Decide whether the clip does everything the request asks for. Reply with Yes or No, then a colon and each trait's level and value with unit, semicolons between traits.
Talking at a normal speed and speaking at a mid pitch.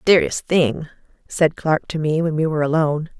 Yes: average, 190 wpm; medium, 155 Hz